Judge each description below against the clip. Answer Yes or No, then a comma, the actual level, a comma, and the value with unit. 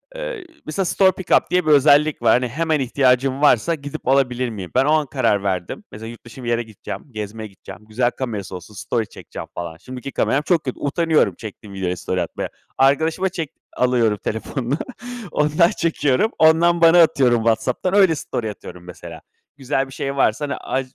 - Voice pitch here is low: Yes, low, 130 Hz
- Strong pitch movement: Yes, wide, 5.7 semitones